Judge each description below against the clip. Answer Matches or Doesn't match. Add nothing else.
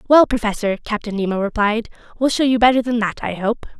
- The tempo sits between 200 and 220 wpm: Matches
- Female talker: Matches